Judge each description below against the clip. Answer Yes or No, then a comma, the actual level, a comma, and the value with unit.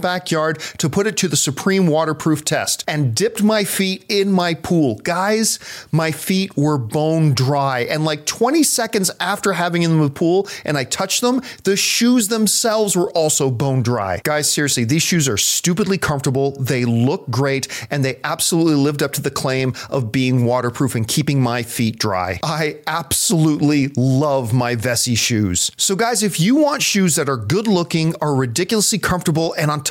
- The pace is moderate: Yes, average, 185 wpm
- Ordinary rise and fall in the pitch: No, wide, 5.8 semitones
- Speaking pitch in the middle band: Yes, medium, 155 Hz